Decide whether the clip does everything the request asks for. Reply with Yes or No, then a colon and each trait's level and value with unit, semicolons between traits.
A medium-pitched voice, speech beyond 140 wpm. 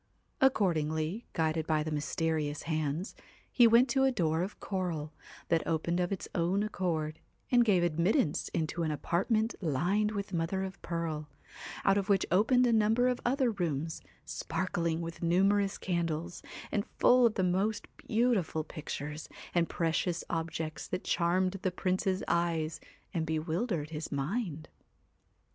Yes: medium, 175 Hz; average, 155 wpm